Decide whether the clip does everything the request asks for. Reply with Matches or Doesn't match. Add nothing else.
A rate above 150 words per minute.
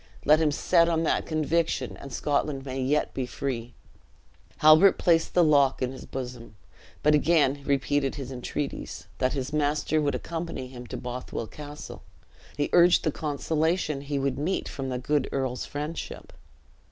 Matches